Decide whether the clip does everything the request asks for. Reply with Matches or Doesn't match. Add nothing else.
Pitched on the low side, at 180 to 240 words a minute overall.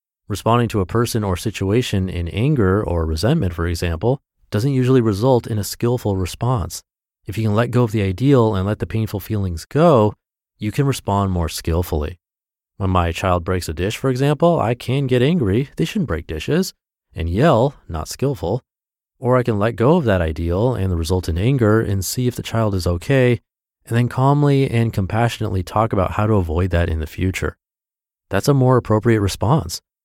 Matches